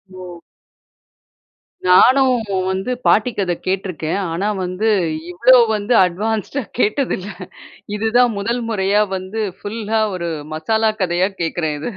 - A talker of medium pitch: No, high, 205 Hz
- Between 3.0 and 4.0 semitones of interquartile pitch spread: Yes, average, 3.6 semitones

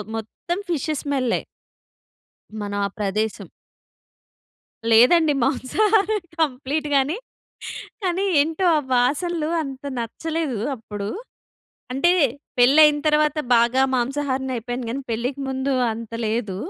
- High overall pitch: Yes, very high, 270 Hz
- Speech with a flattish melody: No, average, 4.5 semitones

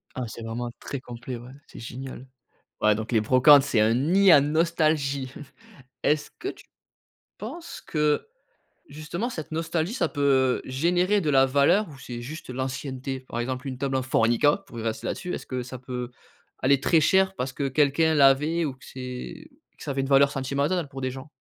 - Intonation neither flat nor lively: Yes, average, 3.3 semitones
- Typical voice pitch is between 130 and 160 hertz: Yes, low, 135 Hz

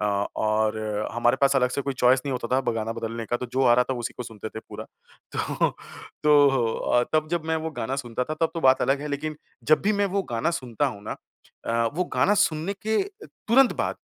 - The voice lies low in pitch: Yes, low, 130 Hz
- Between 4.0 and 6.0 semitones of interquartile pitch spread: Yes, average, 4.8 semitones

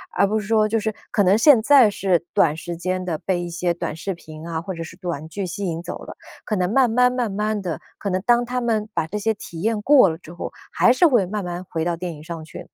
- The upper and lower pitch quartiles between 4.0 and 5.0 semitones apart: Yes, average, 4.3 semitones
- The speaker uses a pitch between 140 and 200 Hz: Yes, high, 190 Hz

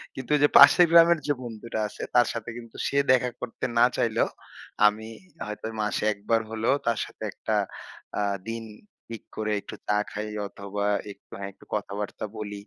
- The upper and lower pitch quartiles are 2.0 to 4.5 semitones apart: Yes, average, 2.7 semitones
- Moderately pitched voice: No, low, 110 Hz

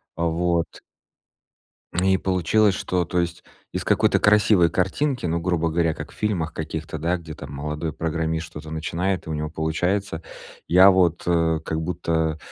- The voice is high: No, very low, 85 Hz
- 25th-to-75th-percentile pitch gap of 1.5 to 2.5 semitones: Yes, narrow, 2.2 semitones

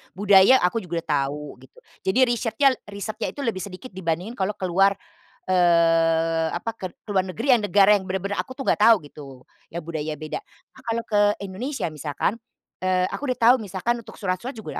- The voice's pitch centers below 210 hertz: Yes, high, 190 Hz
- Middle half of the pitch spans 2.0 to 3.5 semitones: No, average, 4.9 semitones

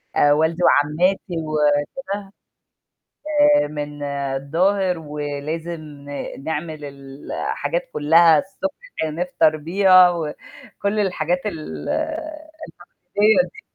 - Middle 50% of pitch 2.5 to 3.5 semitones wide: No, average, 4.6 semitones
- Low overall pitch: No, medium, 160 Hz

